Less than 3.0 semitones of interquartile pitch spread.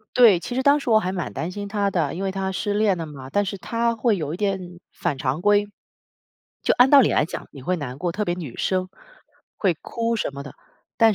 No: average, 4.1 semitones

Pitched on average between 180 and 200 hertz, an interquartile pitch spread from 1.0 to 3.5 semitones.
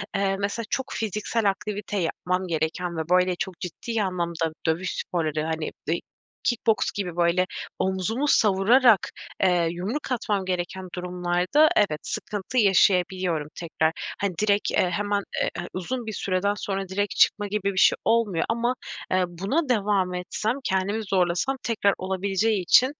Yes: high, 190 Hz; average, 2.9 semitones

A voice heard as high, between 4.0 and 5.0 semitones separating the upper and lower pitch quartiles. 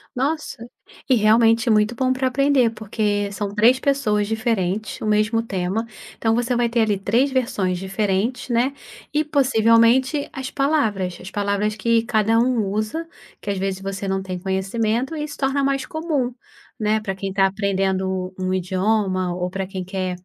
Yes: high, 215 Hz; average, 4.3 semitones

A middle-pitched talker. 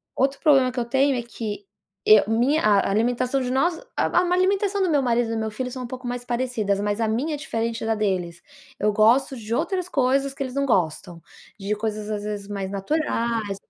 No: high, 235 Hz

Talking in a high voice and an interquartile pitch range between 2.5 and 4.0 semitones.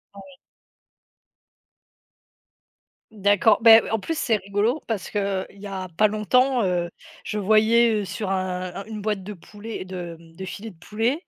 Yes: high, 205 Hz; average, 2.9 semitones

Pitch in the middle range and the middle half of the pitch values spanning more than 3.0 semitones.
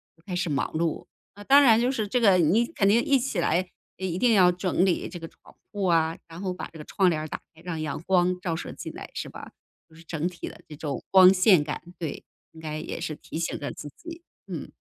Yes: medium, 180 Hz; average, 3.7 semitones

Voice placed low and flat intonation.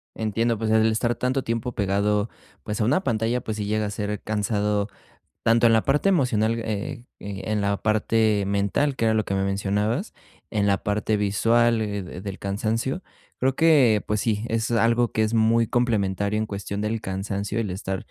Yes: low, 110 Hz; narrow, 2.2 semitones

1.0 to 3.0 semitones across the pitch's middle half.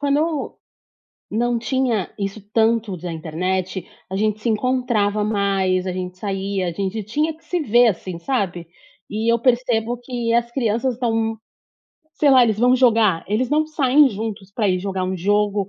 No: average, 4.1 semitones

